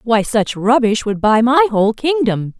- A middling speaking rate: Yes, average, 185 wpm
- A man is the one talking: No, female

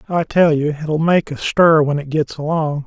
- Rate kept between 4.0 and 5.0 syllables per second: Yes, 4.6 syllables/s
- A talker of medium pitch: Yes, medium, 155 Hz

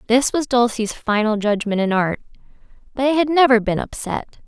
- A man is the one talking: No, female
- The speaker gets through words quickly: No, average, 175 wpm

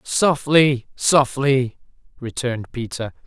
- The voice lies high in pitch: No, low, 130 Hz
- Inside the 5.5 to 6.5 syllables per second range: No, 3.5 syllables/s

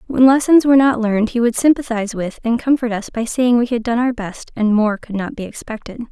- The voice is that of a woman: Yes, female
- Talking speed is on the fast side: Yes, fast, 245 wpm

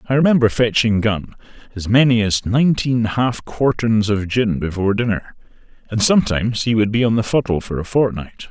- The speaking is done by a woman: No, male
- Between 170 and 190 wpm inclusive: Yes, average, 175 wpm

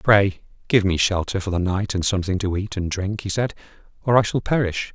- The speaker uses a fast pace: Yes, fast, 230 wpm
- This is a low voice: Yes, low, 100 Hz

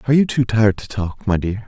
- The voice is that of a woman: No, male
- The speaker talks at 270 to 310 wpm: Yes, fast, 285 wpm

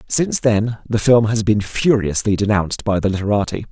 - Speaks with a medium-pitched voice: No, low, 105 Hz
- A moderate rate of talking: Yes, average, 180 wpm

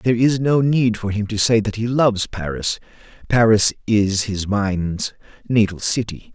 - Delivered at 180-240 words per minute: No, average, 170 wpm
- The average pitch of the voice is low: Yes, low, 105 Hz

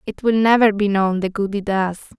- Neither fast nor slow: No, fast, 245 wpm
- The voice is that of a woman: Yes, female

